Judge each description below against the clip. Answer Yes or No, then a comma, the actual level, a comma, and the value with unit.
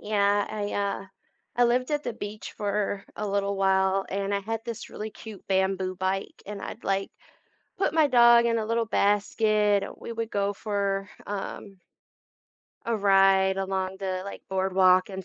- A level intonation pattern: Yes, narrow, 2.0 semitones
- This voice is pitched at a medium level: No, high, 200 Hz